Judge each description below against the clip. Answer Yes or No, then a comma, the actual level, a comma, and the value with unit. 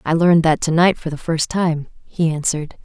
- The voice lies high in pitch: No, medium, 160 Hz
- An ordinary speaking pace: No, fast, 210 wpm